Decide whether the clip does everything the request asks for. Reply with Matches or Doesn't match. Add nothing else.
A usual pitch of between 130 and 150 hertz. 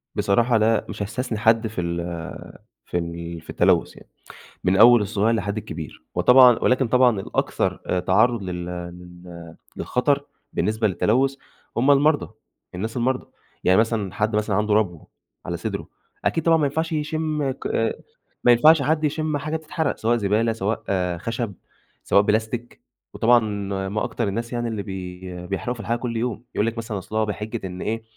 Doesn't match